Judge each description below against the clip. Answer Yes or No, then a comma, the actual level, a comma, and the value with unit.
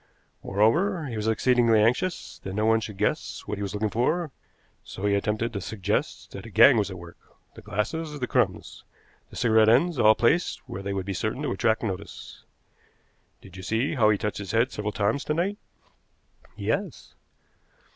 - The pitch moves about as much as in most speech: Yes, average, 3.7 semitones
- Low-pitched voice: Yes, low, 110 Hz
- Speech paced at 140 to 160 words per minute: No, average, 185 wpm